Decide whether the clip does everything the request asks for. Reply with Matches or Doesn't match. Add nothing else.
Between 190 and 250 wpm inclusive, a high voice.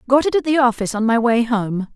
Doesn't match